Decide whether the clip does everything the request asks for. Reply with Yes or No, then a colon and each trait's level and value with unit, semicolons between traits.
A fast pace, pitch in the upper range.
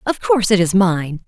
Yes: fast, 235 wpm; high, 200 Hz